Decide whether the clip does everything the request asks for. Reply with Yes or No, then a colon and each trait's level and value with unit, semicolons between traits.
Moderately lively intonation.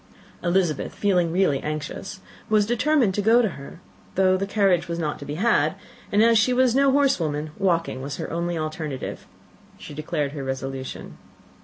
No: wide, 6.0 semitones